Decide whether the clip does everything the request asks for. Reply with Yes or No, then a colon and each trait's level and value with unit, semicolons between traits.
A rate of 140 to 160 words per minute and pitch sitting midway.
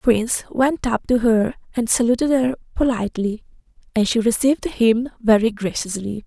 No: average, 155 wpm; high, 235 Hz